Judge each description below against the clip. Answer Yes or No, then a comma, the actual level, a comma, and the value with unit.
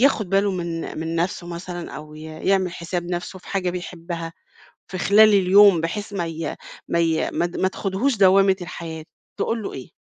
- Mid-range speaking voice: Yes, medium, 180 Hz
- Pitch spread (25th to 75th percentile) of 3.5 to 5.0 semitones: No, average, 2.7 semitones